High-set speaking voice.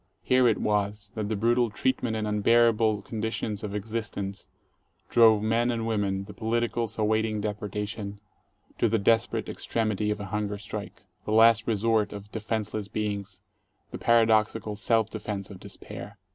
No: low, 110 Hz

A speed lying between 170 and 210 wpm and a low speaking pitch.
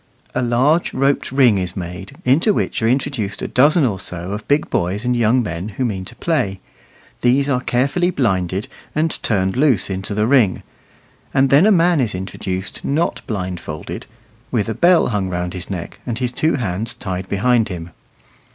Yes: average, 180 wpm; low, 115 Hz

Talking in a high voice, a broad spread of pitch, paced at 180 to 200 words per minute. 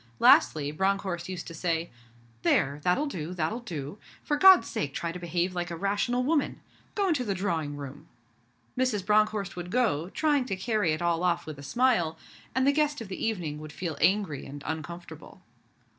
No: medium, 180 Hz; wide, 5.9 semitones; average, 185 wpm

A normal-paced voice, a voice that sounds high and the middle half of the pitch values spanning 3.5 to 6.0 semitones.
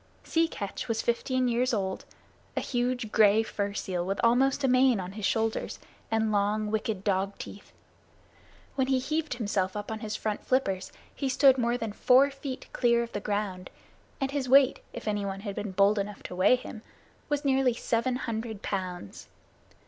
Yes: average, 180 wpm; high, 225 Hz; average, 4.1 semitones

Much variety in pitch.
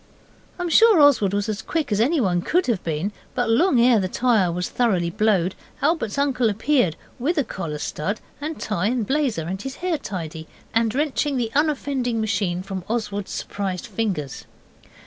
Yes: wide, 6.5 semitones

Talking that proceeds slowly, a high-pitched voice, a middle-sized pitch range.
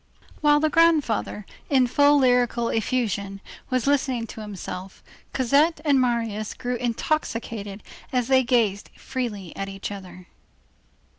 Yes: slow, 125 wpm; high, 240 Hz; average, 4.3 semitones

